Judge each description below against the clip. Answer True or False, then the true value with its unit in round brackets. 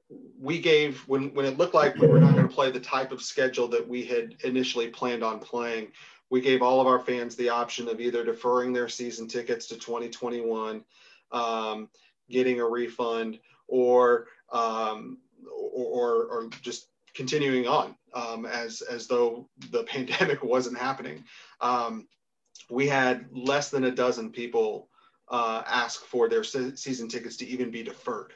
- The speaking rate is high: False (165 wpm)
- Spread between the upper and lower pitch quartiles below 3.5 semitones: True (2.9 semitones)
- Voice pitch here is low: True (125 Hz)